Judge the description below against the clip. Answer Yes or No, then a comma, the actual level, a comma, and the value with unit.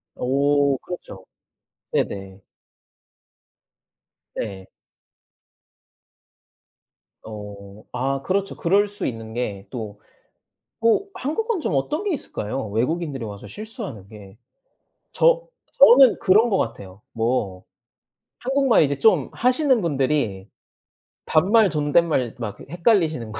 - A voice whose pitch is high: No, medium, 140 Hz